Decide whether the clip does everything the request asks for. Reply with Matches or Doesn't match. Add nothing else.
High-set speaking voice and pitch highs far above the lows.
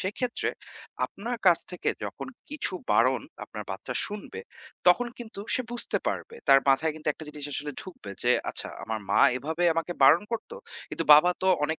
Doesn't match